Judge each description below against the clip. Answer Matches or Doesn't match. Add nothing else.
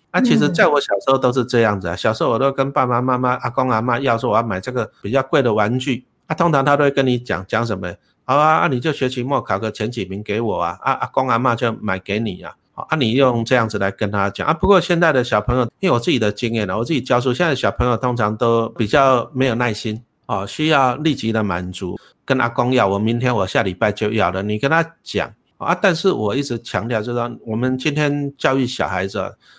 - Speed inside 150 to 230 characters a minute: Doesn't match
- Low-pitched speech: Matches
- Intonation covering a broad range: Doesn't match